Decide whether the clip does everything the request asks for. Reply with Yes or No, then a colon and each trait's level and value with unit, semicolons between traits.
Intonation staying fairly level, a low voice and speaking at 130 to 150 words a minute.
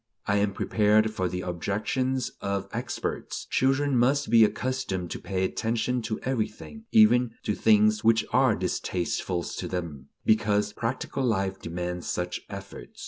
No: average, 4.6 semitones; low, 110 Hz; average, 140 wpm